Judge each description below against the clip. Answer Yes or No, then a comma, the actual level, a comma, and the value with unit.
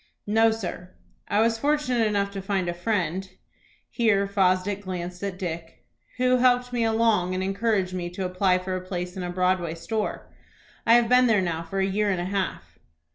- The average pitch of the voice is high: Yes, high, 195 Hz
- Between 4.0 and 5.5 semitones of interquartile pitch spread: No, average, 3.5 semitones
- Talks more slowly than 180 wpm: No, average, 190 wpm